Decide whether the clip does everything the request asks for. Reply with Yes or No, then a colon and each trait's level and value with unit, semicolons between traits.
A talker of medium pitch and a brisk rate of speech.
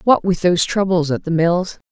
Yes: medium, 180 Hz; fast, 220 wpm